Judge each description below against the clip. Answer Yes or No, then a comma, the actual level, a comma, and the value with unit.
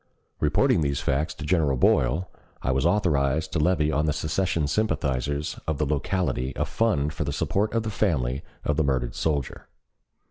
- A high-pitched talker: No, very low, 75 Hz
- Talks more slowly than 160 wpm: No, average, 175 wpm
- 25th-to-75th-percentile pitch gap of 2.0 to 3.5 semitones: No, average, 3.9 semitones